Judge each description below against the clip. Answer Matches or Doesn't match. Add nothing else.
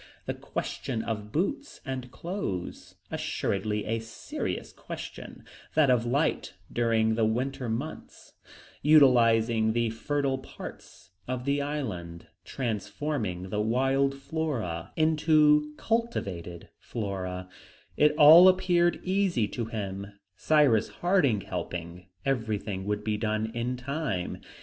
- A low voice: Matches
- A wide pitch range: Matches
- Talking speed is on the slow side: Matches